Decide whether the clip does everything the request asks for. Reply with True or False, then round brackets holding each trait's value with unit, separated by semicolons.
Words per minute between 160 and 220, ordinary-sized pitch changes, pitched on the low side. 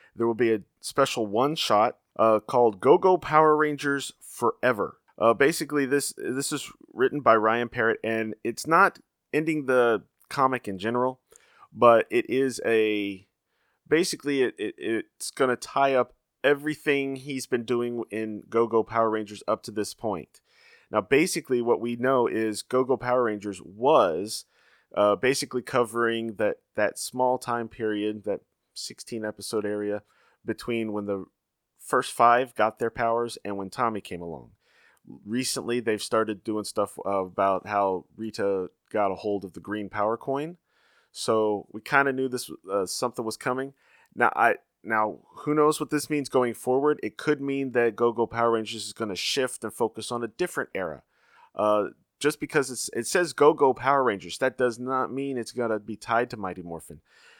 True (175 wpm; 3.8 semitones; 115 Hz)